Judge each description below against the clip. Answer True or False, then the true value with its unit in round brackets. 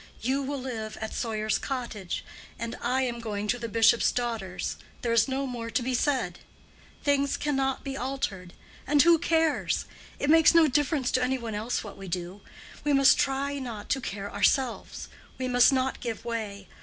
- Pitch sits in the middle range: False (245 Hz)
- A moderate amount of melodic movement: True (3.8 semitones)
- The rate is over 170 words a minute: True (180 wpm)